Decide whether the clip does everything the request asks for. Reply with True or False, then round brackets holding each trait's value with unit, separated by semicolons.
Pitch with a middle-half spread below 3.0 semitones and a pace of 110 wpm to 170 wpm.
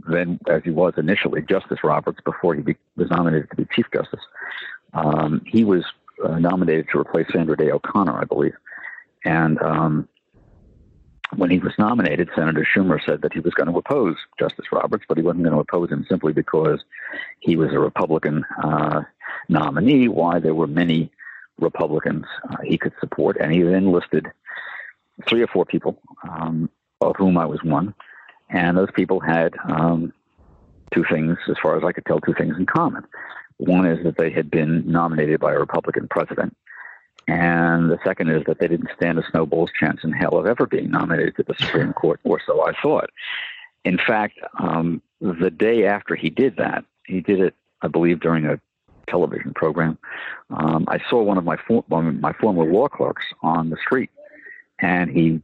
False (2.4 semitones; 185 wpm)